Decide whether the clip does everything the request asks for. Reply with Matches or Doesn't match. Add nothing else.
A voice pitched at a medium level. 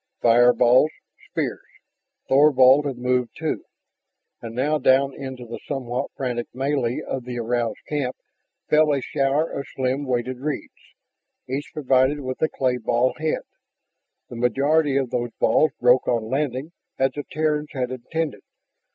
Doesn't match